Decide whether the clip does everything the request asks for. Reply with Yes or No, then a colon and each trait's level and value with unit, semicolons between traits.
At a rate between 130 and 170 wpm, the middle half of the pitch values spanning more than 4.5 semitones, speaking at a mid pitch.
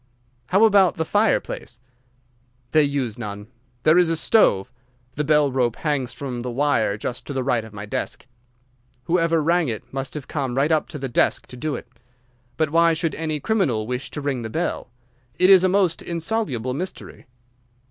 No: average, 185 wpm; average, 5.1 semitones; medium, 145 Hz